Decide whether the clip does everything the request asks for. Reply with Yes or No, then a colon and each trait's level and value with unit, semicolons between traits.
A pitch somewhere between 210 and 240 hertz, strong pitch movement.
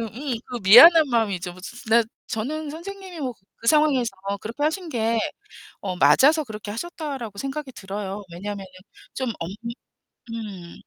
Yes: high, 235 Hz; wide, 6.5 semitones